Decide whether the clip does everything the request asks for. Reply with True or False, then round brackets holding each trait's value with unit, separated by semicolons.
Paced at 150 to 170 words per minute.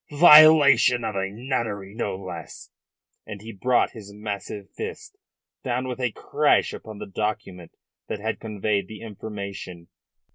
False (140 wpm)